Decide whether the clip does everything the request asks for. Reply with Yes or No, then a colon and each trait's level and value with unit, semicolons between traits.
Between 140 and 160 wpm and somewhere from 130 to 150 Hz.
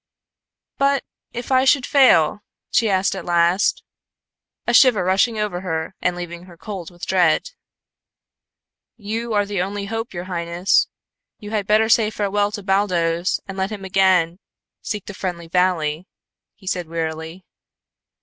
No: average, 150 wpm; high, 190 Hz